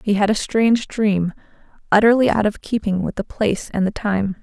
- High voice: Yes, high, 210 Hz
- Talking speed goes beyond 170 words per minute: Yes, fast, 205 wpm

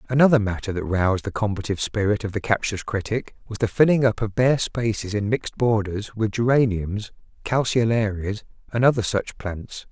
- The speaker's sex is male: Yes, male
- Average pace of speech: Yes, average, 170 wpm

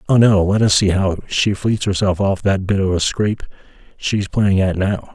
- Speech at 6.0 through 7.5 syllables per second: No, 4.9 syllables/s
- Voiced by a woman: No, male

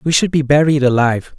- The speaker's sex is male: Yes, male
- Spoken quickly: Yes, fast, 215 wpm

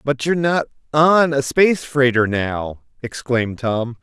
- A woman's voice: No, male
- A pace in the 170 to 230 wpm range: No, average, 150 wpm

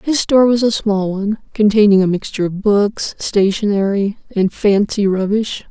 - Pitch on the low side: No, high, 205 Hz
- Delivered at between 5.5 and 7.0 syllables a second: No, 4.9 syllables/s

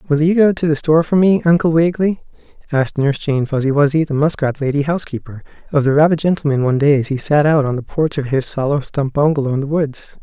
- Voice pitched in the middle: Yes, medium, 150 Hz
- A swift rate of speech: Yes, fast, 235 wpm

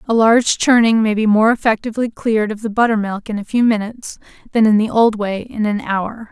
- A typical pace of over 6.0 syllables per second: No, 5.6 syllables/s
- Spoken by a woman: Yes, female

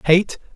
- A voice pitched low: No, medium, 175 Hz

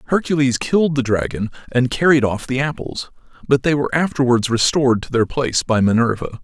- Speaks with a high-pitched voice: No, low, 130 Hz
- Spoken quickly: No, average, 175 wpm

